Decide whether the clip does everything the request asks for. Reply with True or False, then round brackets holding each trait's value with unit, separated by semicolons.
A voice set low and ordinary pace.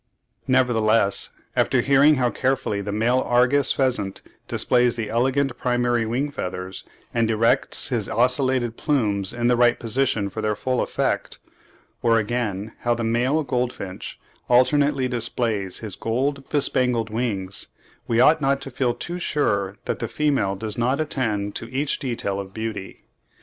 True (120 Hz; 150 wpm)